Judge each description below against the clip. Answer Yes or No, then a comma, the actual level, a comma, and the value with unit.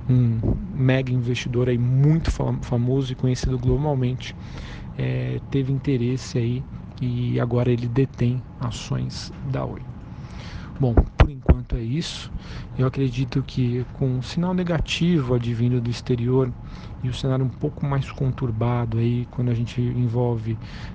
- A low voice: Yes, low, 125 Hz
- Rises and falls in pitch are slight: Yes, narrow, 1.8 semitones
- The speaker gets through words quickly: No, average, 130 wpm